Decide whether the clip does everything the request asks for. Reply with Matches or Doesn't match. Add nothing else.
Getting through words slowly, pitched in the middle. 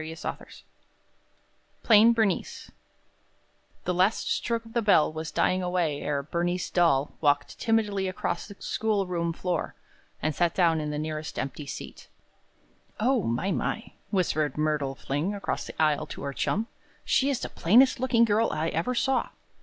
Doesn't match